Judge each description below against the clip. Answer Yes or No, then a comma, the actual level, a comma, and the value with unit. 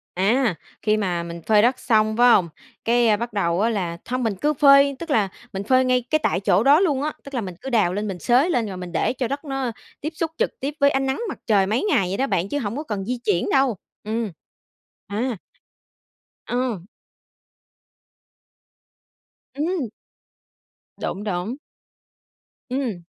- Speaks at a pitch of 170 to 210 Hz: No, high, 235 Hz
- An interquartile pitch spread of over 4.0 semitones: Yes, average, 5.3 semitones